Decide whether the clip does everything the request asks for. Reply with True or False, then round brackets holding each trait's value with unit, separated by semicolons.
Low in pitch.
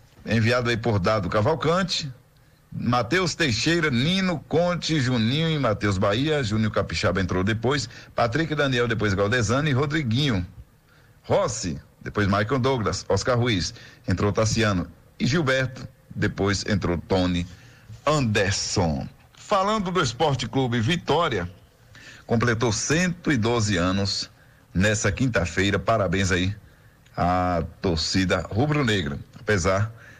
True (115 Hz)